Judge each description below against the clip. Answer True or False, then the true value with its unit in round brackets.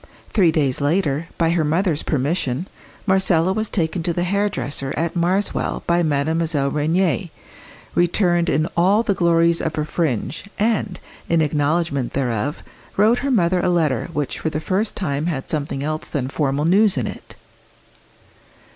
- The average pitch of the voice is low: False (165 Hz)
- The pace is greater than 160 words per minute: False (155 wpm)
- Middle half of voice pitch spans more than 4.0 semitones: False (3.7 semitones)